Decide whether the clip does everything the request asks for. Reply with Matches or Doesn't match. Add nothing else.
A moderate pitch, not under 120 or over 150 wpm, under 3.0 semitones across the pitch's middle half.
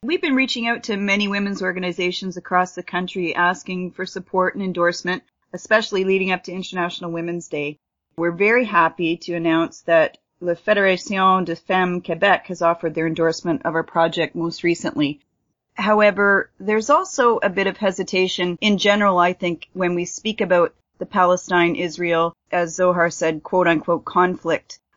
Doesn't match